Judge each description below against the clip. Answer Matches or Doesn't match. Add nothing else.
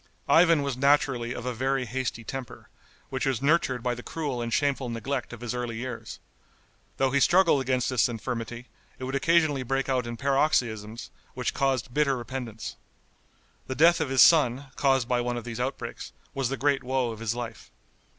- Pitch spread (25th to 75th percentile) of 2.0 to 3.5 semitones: Matches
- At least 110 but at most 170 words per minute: Doesn't match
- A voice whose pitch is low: Matches